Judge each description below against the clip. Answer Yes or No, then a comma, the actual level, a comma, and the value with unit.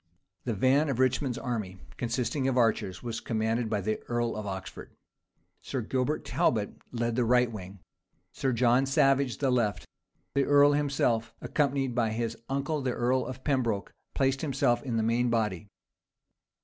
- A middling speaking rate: Yes, average, 160 wpm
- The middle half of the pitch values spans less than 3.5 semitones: Yes, average, 3.0 semitones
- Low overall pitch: Yes, low, 120 Hz